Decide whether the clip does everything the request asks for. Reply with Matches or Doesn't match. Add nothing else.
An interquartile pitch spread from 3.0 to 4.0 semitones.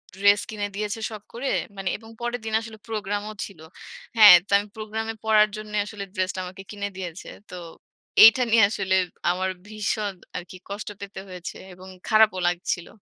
Doesn't match